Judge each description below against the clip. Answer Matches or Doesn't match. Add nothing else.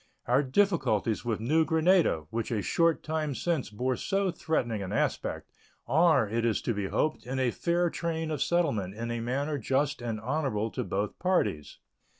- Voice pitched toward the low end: Matches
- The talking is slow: Doesn't match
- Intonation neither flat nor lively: Doesn't match